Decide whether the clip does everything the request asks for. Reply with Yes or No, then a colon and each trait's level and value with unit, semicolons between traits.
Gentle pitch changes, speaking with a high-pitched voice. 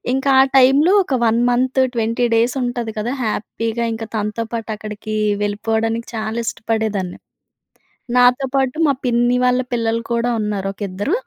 Yes: narrow, 2.2 semitones; high, 230 Hz